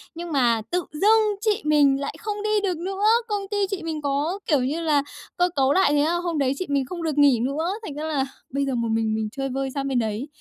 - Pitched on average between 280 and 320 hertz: Yes, very high, 295 Hz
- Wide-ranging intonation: No, average, 4.9 semitones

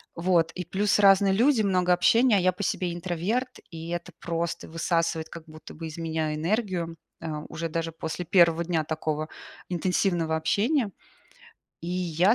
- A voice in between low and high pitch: Yes, medium, 175 Hz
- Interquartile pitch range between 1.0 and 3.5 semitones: Yes, average, 2.8 semitones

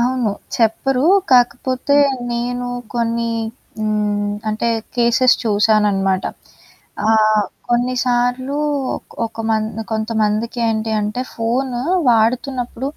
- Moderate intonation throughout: No, narrow, 2.3 semitones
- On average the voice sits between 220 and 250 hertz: Yes, high, 235 Hz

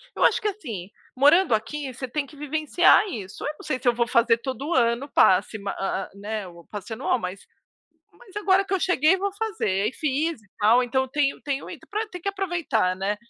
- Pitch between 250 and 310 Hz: Yes, very high, 265 Hz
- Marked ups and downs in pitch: Yes, wide, 7.6 semitones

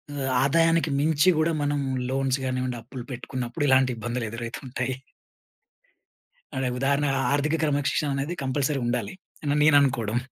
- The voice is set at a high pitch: No, low, 135 Hz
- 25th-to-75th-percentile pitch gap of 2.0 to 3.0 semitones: Yes, narrow, 2.5 semitones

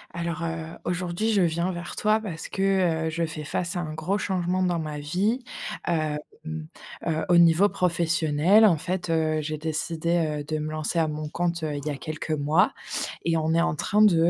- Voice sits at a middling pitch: Yes, medium, 165 Hz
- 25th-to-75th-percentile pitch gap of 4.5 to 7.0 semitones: No, narrow, 2.4 semitones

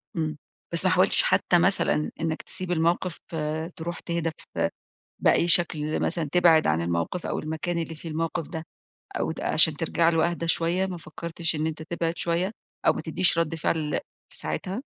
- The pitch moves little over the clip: Yes, narrow, 1.5 semitones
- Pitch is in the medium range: Yes, medium, 165 Hz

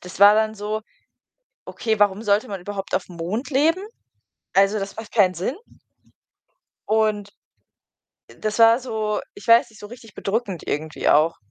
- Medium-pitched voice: No, high, 210 Hz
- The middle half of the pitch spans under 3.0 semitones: Yes, narrow, 2.4 semitones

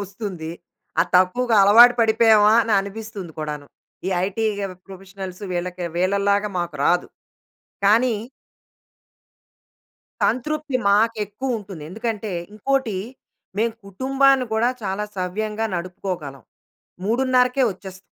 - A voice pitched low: No, high, 210 Hz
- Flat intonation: No, average, 3.7 semitones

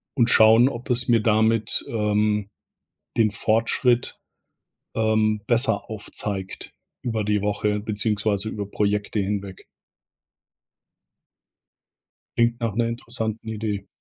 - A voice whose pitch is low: Yes, low, 110 Hz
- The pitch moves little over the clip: Yes, narrow, 1.8 semitones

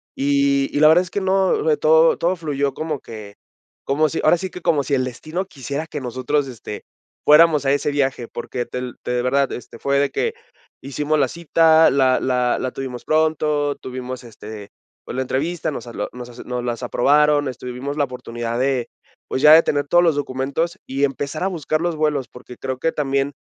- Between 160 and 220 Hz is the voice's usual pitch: No, medium, 140 Hz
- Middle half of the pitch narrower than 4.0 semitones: Yes, average, 3.4 semitones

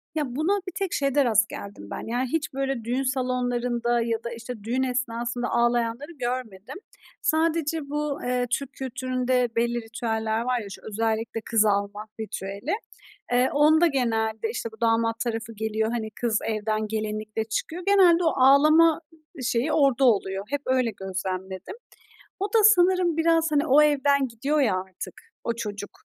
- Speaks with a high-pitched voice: Yes, high, 240 Hz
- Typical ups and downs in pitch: Yes, average, 4.2 semitones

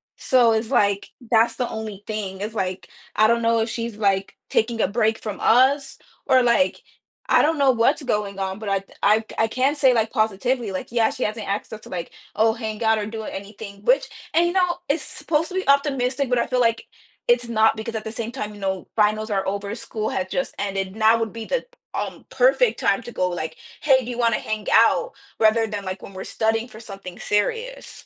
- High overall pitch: Yes, high, 220 Hz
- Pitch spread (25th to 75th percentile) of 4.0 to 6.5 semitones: No, average, 3.1 semitones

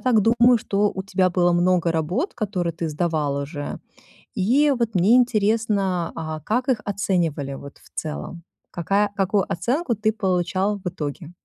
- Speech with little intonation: No, average, 4.2 semitones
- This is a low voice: No, high, 190 Hz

